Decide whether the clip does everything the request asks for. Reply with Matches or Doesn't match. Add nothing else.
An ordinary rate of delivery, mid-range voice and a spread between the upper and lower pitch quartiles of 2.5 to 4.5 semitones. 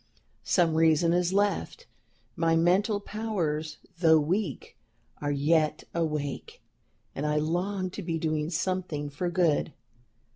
Doesn't match